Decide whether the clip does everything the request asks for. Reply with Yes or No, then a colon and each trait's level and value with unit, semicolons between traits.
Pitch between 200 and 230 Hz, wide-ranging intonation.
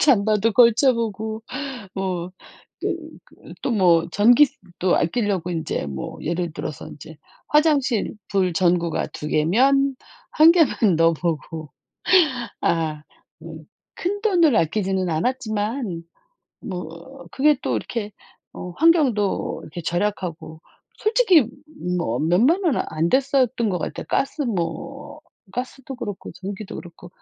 Yes: high, 205 Hz; wide, 7.7 semitones